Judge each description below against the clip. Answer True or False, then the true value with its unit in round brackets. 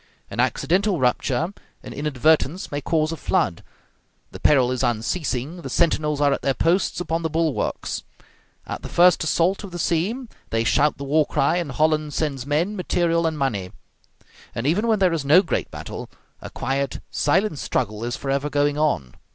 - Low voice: False (150 Hz)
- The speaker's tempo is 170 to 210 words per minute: True (175 wpm)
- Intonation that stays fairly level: False (3.8 semitones)